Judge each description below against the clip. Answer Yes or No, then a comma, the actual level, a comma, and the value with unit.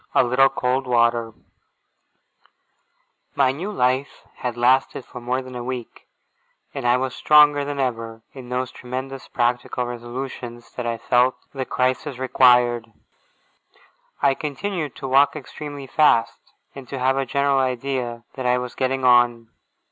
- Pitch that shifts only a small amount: Yes, narrow, 1.9 semitones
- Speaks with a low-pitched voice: Yes, low, 130 Hz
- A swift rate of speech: No, average, 145 wpm